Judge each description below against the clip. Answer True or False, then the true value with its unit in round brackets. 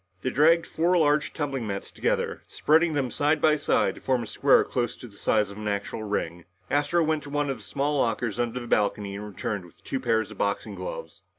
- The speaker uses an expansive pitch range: True (5.9 semitones)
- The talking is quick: True (225 wpm)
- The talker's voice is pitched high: False (130 Hz)